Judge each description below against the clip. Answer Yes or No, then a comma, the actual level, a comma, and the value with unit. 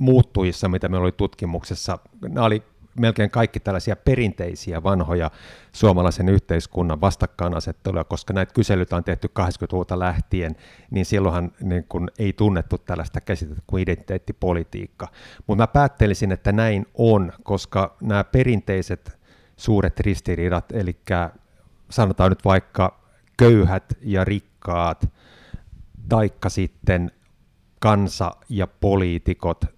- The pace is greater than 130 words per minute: No, average, 110 wpm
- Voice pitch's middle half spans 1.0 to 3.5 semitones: Yes, average, 3.2 semitones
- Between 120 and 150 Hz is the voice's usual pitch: No, very low, 95 Hz